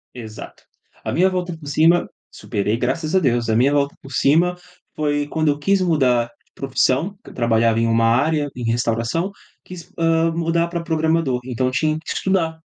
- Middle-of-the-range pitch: Yes, medium, 145 Hz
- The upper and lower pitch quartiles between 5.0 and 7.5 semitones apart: Yes, average, 5.3 semitones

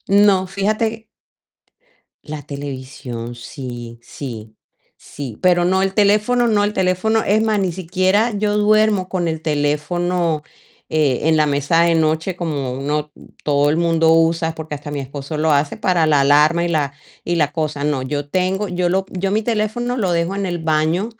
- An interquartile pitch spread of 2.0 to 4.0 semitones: No, average, 4.6 semitones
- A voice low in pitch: No, medium, 165 Hz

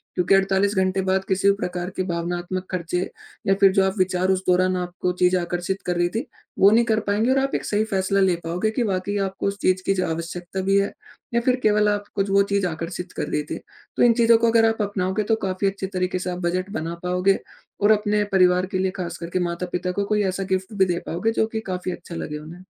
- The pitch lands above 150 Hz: Yes, high, 190 Hz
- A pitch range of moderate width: No, narrow, 2.1 semitones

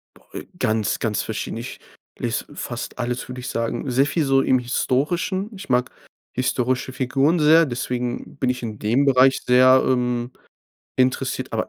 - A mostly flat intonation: Yes, narrow, 1.8 semitones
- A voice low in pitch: Yes, low, 125 Hz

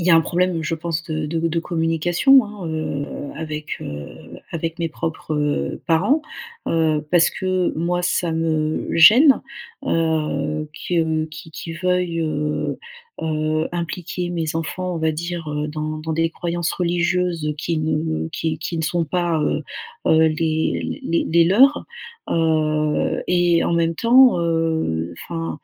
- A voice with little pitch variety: Yes, narrow, 1.9 semitones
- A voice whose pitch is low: No, medium, 165 Hz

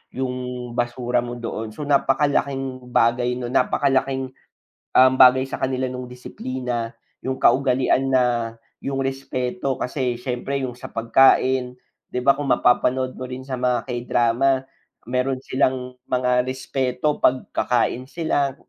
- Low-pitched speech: Yes, low, 130 Hz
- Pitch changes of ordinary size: No, narrow, 1.2 semitones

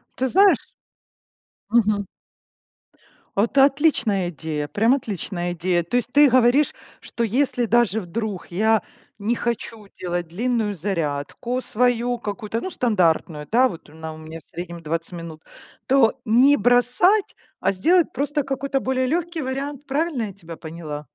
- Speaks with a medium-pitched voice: No, high, 225 Hz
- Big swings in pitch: Yes, wide, 6.9 semitones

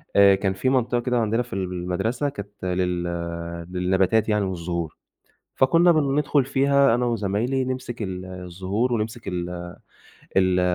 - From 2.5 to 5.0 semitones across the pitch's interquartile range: No, wide, 5.5 semitones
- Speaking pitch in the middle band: No, low, 105 Hz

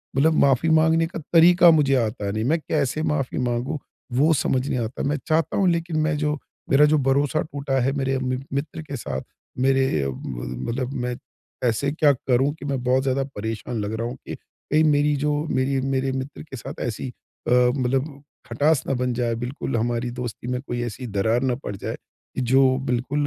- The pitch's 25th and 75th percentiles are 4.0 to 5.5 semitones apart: No, average, 3.3 semitones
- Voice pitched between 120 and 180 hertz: Yes, low, 135 Hz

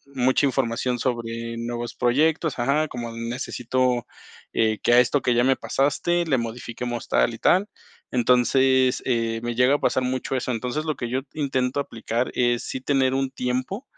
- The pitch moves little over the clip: Yes, narrow, 2.1 semitones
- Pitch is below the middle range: Yes, low, 125 Hz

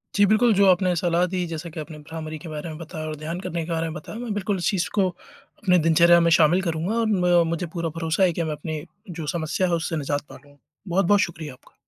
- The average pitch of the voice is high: No, medium, 170 Hz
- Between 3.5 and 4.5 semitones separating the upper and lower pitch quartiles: No, narrow, 2.5 semitones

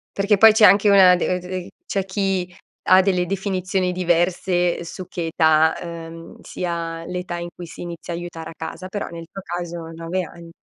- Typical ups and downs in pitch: No, narrow, 1.8 semitones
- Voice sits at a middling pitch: Yes, medium, 180 Hz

